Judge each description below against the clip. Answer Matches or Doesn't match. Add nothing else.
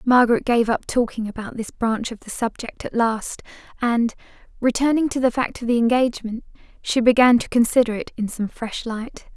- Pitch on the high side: Matches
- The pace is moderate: Matches